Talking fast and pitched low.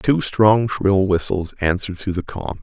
No: average, 185 wpm; low, 100 Hz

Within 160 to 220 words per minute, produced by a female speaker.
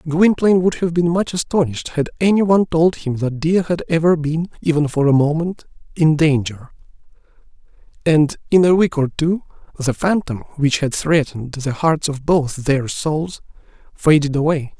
No: average, 165 wpm; male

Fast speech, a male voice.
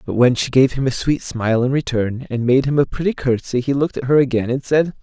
Yes: fast, 275 wpm; male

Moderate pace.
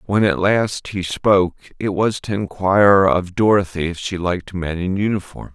Yes: average, 185 wpm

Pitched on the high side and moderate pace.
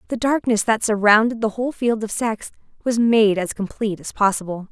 Yes: high, 220 Hz; average, 190 wpm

